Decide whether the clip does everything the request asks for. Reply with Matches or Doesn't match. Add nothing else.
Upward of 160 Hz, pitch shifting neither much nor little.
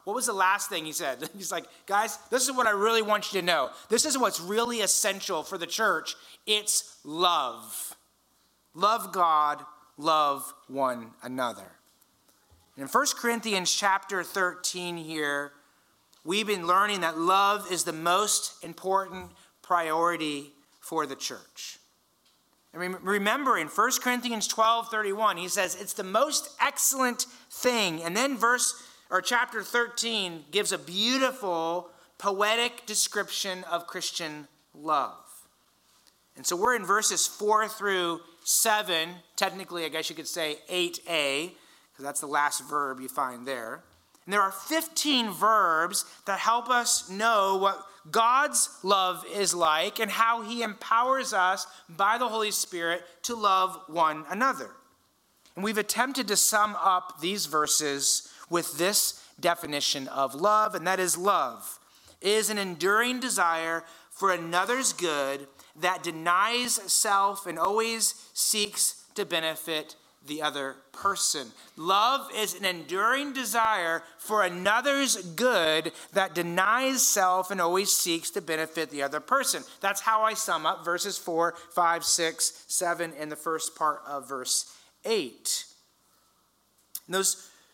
Matches